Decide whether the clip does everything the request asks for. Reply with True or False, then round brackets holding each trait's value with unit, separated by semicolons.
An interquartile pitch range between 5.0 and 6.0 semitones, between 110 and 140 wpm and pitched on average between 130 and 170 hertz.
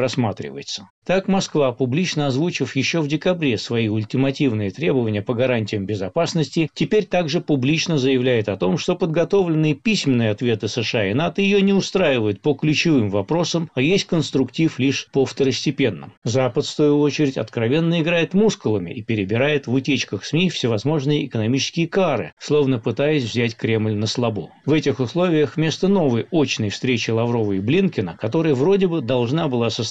False (5.6 semitones; 155 wpm; 140 Hz)